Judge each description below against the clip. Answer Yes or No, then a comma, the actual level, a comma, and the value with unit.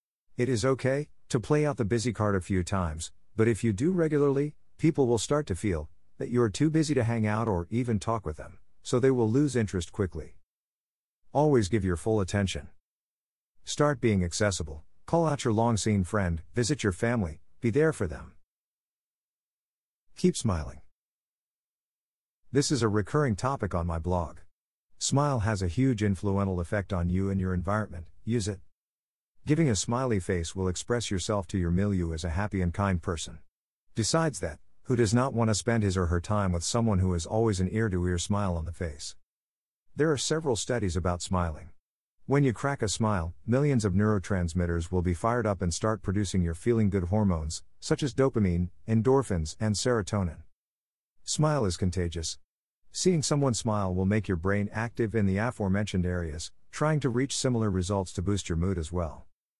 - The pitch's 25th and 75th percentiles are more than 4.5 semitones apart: Yes, average, 5.1 semitones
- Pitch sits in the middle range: No, low, 105 Hz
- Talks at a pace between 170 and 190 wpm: Yes, average, 180 wpm